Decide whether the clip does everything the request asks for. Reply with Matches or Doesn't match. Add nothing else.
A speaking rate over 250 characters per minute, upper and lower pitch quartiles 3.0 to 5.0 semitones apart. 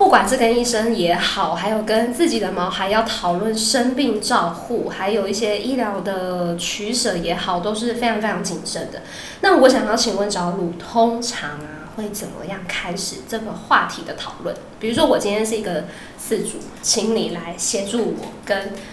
Matches